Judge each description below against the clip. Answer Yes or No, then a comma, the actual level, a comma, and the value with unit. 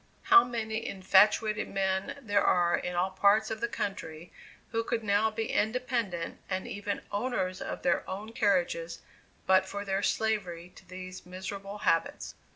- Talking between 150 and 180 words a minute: Yes, average, 155 wpm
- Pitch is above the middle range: Yes, high, 200 Hz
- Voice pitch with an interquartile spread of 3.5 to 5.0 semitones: No, average, 2.9 semitones